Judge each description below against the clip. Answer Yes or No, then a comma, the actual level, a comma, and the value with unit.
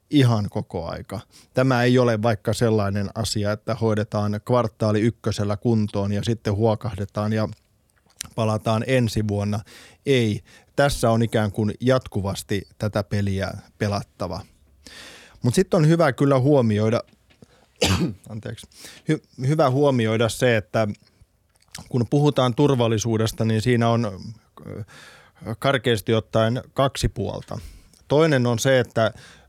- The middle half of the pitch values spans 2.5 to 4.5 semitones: Yes, average, 2.9 semitones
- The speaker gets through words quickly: No, average, 115 wpm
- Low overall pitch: Yes, low, 110 Hz